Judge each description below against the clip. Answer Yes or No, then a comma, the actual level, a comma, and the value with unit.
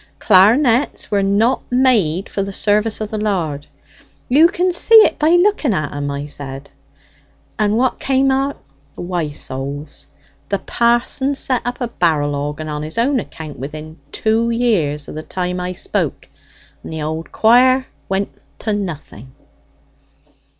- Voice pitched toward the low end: No, high, 200 Hz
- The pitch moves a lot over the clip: Yes, wide, 8.2 semitones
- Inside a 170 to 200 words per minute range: No, average, 150 wpm